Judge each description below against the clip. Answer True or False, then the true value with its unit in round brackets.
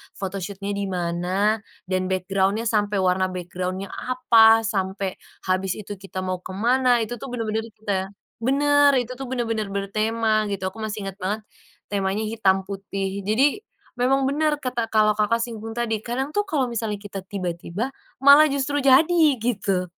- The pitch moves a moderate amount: True (4.0 semitones)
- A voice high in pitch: True (215 Hz)